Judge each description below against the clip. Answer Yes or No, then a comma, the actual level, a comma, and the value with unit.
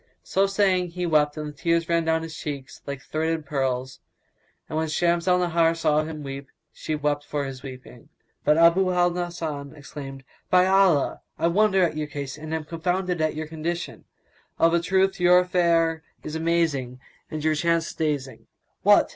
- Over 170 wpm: Yes, average, 180 wpm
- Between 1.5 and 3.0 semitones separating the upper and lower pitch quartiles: Yes, average, 2.7 semitones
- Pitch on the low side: No, medium, 160 Hz